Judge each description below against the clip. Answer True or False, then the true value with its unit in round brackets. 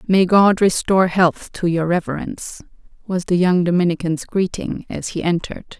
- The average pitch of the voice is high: False (180 Hz)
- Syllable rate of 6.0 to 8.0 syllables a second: False (5.1 syllables/s)